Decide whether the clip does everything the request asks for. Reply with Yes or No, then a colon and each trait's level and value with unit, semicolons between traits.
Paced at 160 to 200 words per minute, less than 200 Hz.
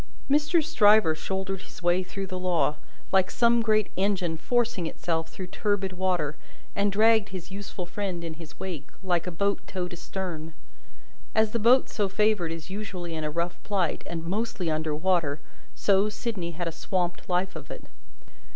Yes: average, 170 wpm; medium, 185 Hz